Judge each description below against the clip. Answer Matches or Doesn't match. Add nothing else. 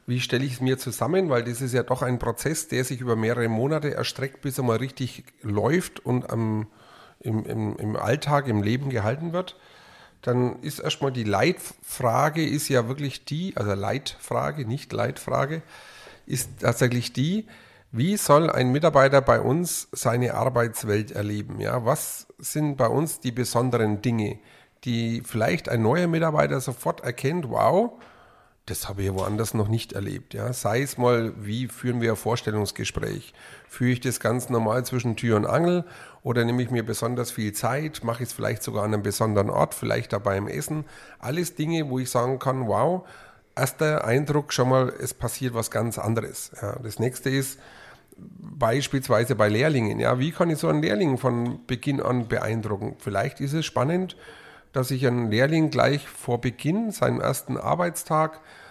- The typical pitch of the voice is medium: Doesn't match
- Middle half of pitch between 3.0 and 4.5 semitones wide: Matches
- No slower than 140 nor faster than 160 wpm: Doesn't match